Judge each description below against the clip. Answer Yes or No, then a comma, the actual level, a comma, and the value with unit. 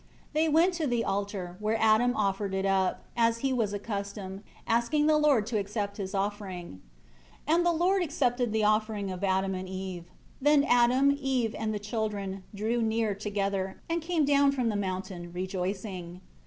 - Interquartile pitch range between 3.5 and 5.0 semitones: Yes, average, 4.5 semitones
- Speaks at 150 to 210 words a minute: Yes, average, 175 wpm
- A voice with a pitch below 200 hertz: No, high, 215 Hz